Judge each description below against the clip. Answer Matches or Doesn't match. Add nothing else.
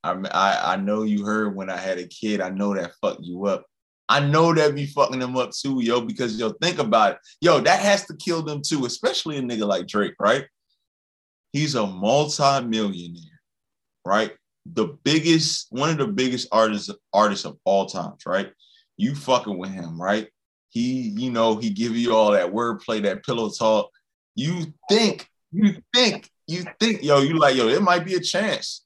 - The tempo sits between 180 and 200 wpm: Matches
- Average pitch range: Doesn't match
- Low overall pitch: Matches